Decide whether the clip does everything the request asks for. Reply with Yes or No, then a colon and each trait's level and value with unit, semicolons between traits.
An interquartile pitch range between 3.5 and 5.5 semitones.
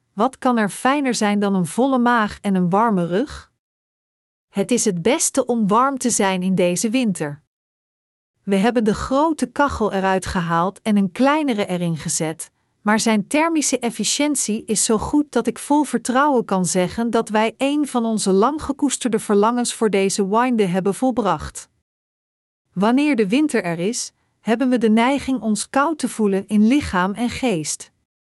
Yes: average, 4.3 semitones